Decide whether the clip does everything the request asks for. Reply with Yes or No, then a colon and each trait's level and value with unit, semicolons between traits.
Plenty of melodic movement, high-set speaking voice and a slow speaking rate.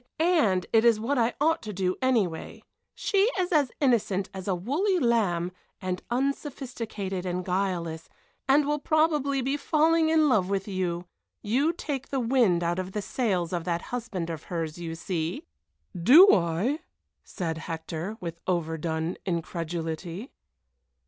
No: wide, 7.8 semitones; high, 195 Hz; average, 150 wpm